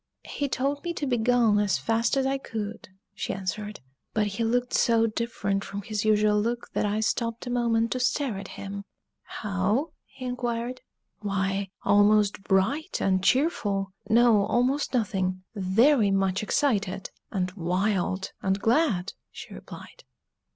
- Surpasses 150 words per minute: No, average, 145 wpm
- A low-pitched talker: No, high, 215 Hz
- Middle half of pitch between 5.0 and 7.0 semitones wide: No, average, 3.7 semitones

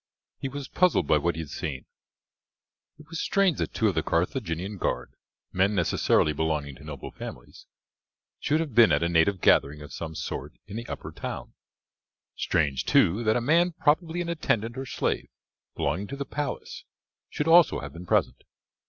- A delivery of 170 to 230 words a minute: Yes, average, 180 wpm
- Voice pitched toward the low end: Yes, low, 100 Hz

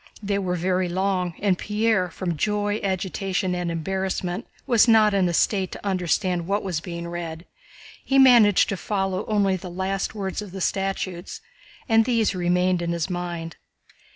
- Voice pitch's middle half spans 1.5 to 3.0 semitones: Yes, narrow, 2.6 semitones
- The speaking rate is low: No, average, 165 wpm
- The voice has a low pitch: No, high, 190 Hz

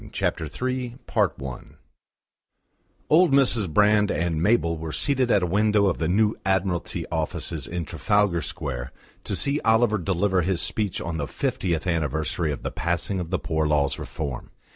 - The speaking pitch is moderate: No, very low, 90 Hz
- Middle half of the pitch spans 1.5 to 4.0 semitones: No, average, 4.7 semitones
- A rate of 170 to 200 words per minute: No, average, 160 wpm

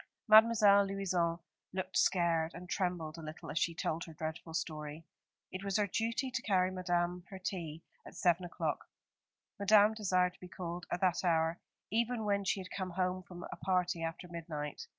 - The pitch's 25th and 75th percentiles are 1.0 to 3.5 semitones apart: Yes, average, 2.8 semitones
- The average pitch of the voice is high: No, medium, 180 Hz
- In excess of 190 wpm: No, average, 180 wpm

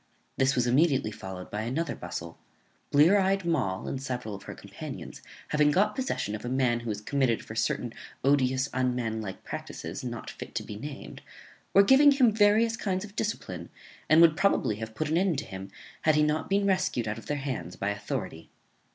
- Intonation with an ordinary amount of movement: No, wide, 8.8 semitones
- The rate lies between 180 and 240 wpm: Yes, average, 195 wpm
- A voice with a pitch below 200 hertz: Yes, low, 135 Hz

